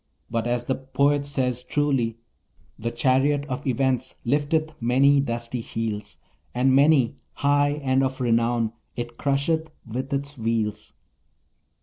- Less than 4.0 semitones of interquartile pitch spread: Yes, average, 3.2 semitones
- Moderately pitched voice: No, low, 130 Hz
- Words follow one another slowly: Yes, slow, 125 wpm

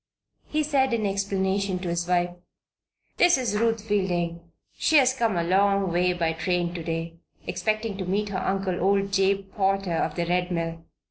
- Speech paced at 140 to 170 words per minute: No, average, 180 wpm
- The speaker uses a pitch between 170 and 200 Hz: Yes, high, 190 Hz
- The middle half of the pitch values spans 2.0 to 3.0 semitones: Yes, average, 2.7 semitones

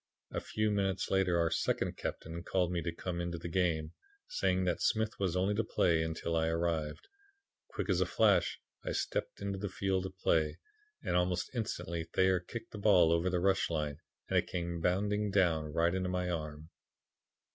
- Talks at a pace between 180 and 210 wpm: Yes, average, 190 wpm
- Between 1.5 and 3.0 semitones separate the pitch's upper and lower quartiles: Yes, narrow, 2.6 semitones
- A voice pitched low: Yes, very low, 90 Hz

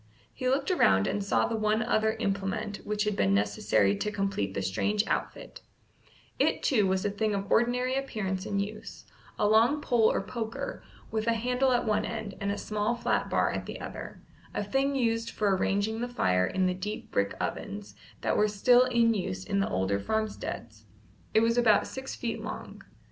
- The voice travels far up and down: No, average, 3.1 semitones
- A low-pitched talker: No, high, 210 Hz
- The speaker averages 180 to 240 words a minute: Yes, average, 190 wpm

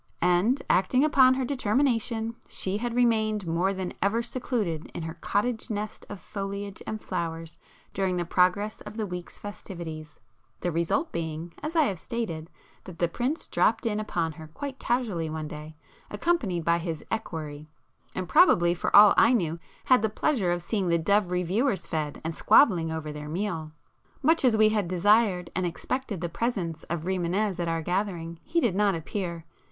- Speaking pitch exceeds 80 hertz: Yes, high, 190 Hz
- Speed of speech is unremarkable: Yes, average, 175 wpm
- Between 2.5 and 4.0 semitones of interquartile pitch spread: No, average, 4.9 semitones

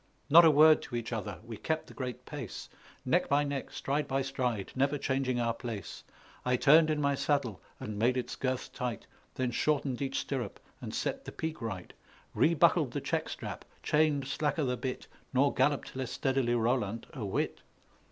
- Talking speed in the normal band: Yes, average, 180 wpm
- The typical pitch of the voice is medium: No, low, 130 Hz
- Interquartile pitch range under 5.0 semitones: Yes, average, 3.0 semitones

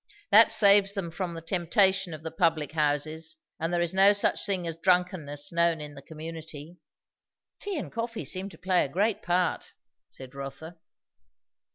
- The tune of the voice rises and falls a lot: No, average, 3.3 semitones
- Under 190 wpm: Yes, average, 170 wpm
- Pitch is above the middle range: No, medium, 170 Hz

